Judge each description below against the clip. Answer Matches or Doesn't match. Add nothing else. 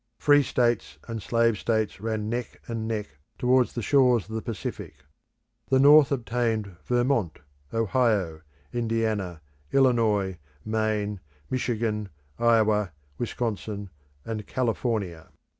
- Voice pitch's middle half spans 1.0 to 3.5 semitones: Matches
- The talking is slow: Matches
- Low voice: Matches